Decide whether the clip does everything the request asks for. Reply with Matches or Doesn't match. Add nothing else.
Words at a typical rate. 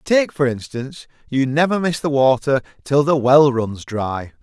Matches